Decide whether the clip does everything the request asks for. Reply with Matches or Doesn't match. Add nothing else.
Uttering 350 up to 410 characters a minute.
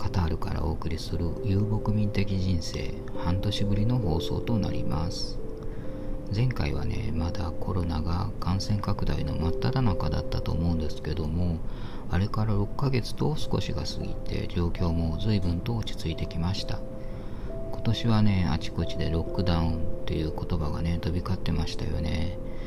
Doesn't match